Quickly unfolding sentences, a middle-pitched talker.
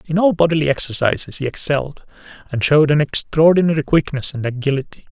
No: average, 150 wpm; medium, 150 Hz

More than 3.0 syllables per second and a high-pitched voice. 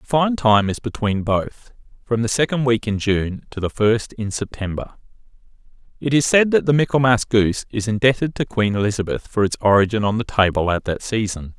No: 5.3 syllables/s; low, 115 Hz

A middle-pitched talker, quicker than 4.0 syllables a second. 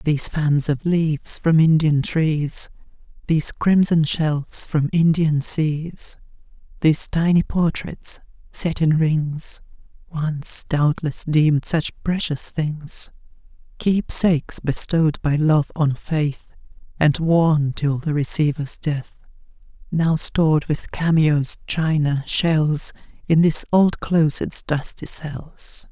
No: medium, 155 Hz; 3.4 syllables/s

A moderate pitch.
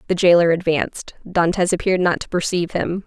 Yes: medium, 175 Hz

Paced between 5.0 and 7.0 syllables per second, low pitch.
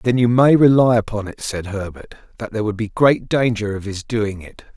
Yes: 5.1 syllables/s; low, 110 Hz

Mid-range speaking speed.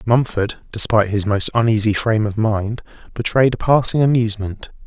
Yes: average, 150 wpm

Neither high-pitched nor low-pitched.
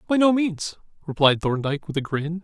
Yes: medium, 165 Hz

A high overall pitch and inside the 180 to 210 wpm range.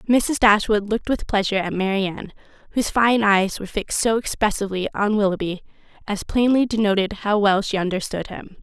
No: high, 210 Hz; average, 165 wpm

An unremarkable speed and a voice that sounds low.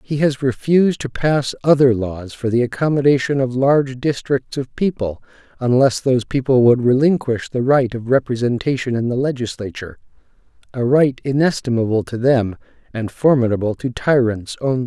Yes: average, 150 wpm; low, 125 Hz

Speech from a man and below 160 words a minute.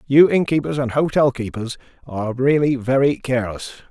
Yes: male; average, 140 wpm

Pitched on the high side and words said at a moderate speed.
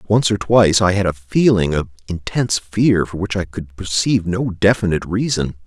No: very low, 95 Hz; average, 190 wpm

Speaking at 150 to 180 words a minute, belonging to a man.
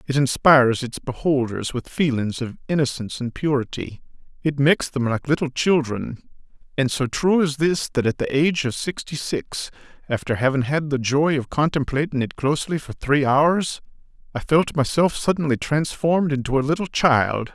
Yes: average, 170 wpm; male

